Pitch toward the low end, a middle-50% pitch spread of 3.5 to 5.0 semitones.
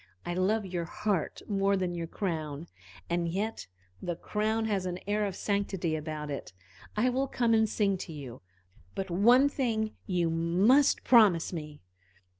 No: high, 190 Hz; average, 4.4 semitones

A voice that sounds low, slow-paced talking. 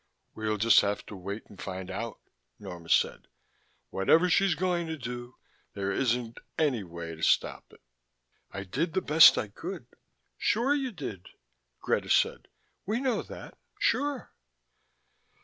No: low, 120 Hz; average, 150 wpm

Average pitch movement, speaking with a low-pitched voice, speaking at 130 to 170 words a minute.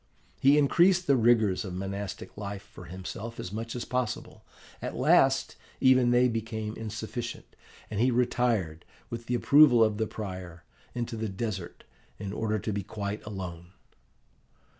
Yes: average, 3.6 semitones; low, 110 Hz; average, 150 wpm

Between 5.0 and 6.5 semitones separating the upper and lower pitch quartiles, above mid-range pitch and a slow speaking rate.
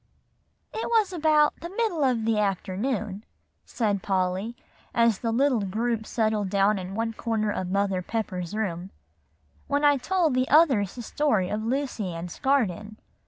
No: wide, 5.4 semitones; high, 220 Hz; average, 155 wpm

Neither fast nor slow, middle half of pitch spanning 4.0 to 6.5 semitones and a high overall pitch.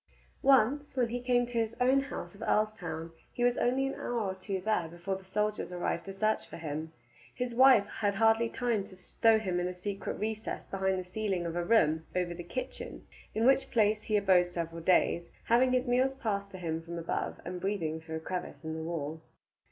No: fast, 215 wpm; average, 5.0 semitones; high, 200 Hz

